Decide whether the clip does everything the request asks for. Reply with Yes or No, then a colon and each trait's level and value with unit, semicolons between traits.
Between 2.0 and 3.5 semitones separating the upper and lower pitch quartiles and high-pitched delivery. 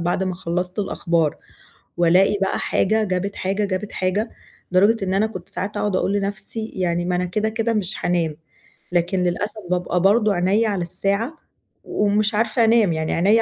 Yes: average, 3.0 semitones; high, 195 Hz